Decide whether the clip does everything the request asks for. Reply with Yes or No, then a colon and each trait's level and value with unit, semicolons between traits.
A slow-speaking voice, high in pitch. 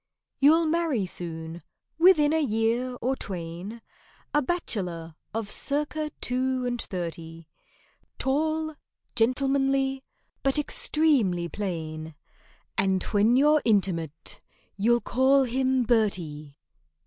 Yes: slow, 95 wpm; high, 240 Hz